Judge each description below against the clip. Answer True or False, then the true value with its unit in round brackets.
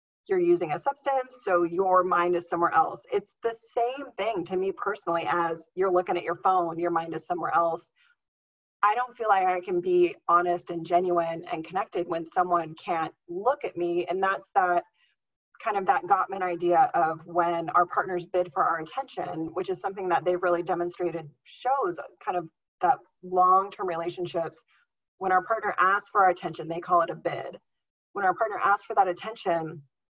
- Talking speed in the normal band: True (185 wpm)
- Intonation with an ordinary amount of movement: True (3.3 semitones)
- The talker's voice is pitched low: False (180 Hz)